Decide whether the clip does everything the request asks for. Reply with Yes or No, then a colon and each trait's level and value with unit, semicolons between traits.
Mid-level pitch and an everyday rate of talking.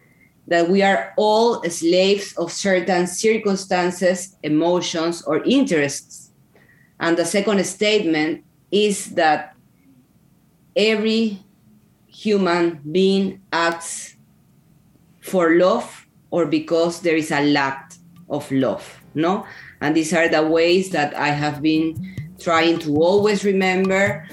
No: medium, 170 Hz; slow, 110 wpm